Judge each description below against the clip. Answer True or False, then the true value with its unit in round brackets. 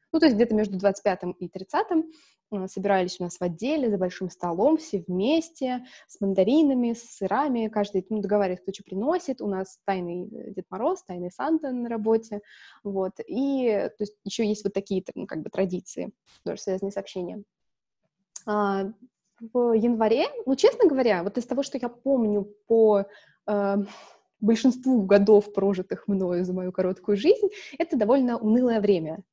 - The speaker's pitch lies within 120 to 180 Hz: False (210 Hz)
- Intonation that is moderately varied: True (4.5 semitones)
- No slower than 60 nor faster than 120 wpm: False (160 wpm)